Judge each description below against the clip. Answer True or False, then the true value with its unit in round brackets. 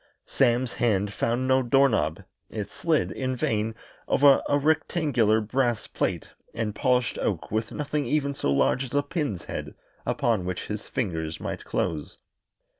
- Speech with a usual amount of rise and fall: True (4.7 semitones)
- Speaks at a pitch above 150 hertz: False (120 Hz)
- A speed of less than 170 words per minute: True (155 wpm)